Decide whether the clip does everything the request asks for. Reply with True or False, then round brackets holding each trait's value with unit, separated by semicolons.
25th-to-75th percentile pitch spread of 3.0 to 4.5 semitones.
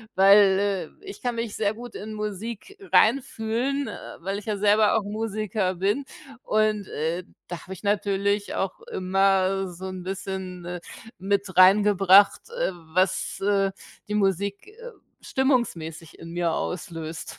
False (2.6 semitones)